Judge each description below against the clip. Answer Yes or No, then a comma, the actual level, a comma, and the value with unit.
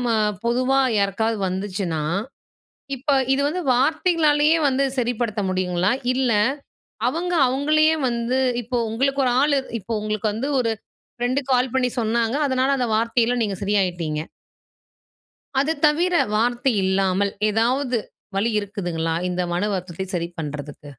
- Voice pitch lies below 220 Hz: No, high, 230 Hz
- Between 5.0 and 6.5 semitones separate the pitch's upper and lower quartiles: Yes, average, 5.3 semitones